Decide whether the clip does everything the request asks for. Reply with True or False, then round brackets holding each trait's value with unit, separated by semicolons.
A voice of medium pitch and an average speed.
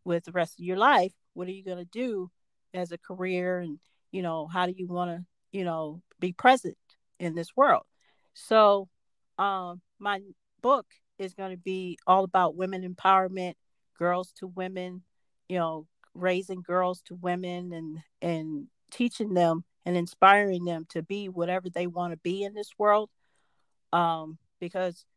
True (180 Hz; 165 wpm)